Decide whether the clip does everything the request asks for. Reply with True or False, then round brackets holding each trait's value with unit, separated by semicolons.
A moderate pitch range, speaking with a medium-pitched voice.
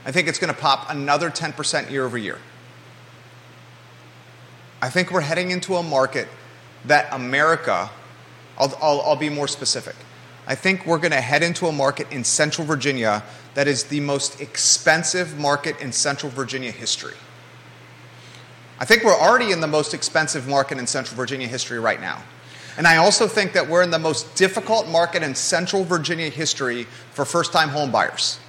True (3.9 semitones; 145 Hz)